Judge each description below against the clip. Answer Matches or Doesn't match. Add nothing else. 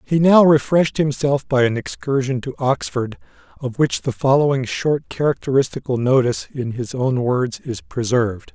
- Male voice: Matches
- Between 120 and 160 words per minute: Matches